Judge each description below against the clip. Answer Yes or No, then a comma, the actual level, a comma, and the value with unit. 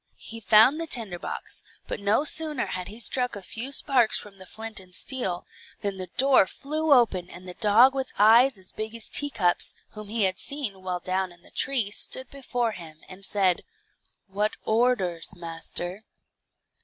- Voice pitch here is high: Yes, high, 215 Hz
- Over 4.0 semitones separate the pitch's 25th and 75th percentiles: Yes, average, 5.1 semitones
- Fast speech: No, average, 180 wpm